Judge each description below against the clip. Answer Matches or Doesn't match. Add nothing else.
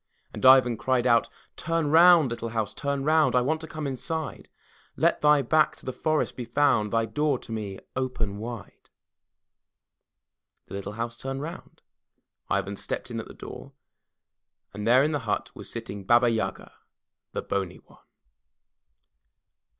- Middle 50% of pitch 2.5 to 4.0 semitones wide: Doesn't match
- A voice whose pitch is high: Doesn't match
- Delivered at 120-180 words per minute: Matches